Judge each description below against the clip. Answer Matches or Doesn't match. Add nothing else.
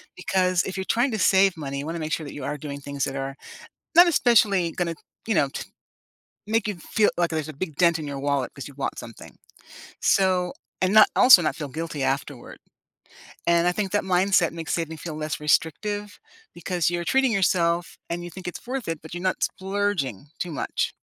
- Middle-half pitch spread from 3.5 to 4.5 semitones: Matches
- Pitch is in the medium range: Matches